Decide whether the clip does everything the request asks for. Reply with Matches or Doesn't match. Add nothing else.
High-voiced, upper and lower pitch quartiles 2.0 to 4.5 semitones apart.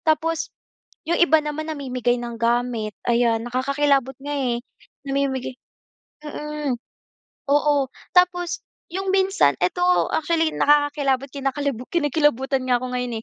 Matches